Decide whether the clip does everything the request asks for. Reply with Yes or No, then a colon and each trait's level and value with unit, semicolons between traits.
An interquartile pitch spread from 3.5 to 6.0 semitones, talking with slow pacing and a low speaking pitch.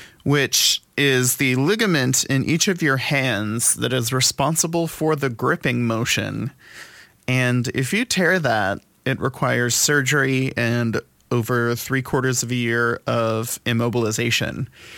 No: narrow, 2.6 semitones; slow, 130 wpm; low, 125 Hz